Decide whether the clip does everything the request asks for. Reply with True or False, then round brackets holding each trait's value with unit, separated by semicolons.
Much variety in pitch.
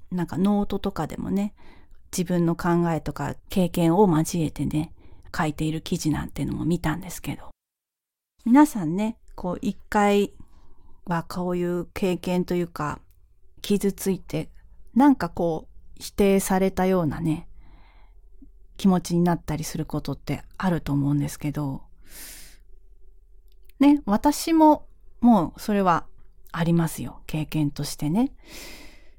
False (4.7 semitones)